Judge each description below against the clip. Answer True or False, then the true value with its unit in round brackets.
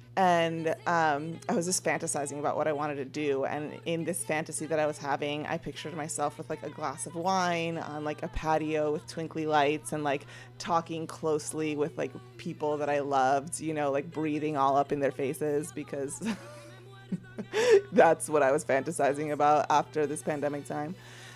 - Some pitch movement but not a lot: False (1.9 semitones)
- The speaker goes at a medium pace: True (185 wpm)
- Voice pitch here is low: False (150 Hz)